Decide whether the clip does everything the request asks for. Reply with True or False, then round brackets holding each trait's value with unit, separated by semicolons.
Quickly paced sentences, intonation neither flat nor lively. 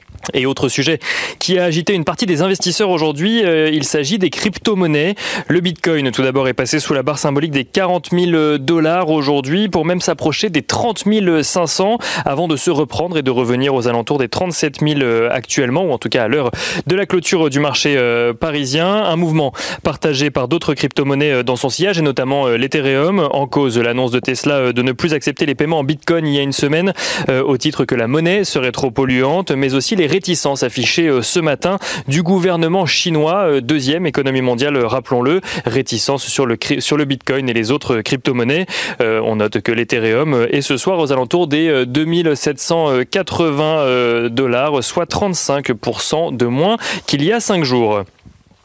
False (185 wpm; 4.6 semitones)